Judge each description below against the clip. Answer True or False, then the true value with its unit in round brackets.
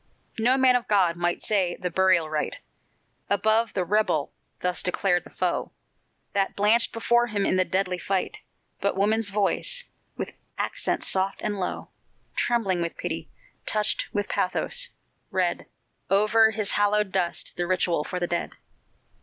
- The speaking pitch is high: True (195 Hz)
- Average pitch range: True (3.1 semitones)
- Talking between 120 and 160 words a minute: True (150 wpm)